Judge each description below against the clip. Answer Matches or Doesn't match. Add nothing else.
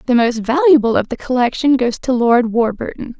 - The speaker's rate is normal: Matches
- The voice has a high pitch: Matches